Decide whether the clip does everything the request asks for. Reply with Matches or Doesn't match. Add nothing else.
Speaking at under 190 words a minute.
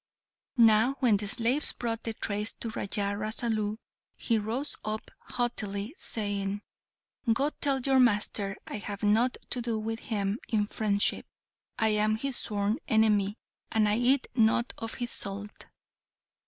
Matches